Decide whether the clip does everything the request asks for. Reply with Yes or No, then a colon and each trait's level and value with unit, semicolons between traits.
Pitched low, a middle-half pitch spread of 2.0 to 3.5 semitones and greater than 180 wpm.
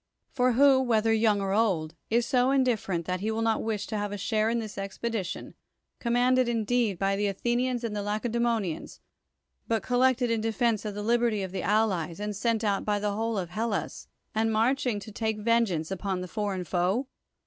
No: high, 220 Hz; average, 2.9 semitones; average, 190 wpm